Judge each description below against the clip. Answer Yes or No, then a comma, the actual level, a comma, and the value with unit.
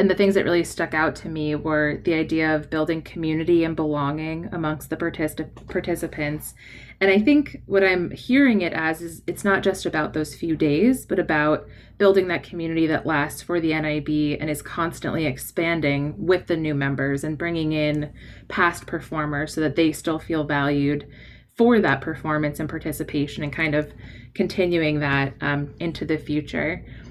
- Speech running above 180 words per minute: No, average, 175 wpm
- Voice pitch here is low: No, medium, 155 Hz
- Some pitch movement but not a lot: No, narrow, 2.3 semitones